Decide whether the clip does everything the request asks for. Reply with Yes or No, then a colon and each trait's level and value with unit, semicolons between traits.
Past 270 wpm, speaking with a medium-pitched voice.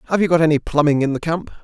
Yes: fast, 295 wpm; medium, 155 Hz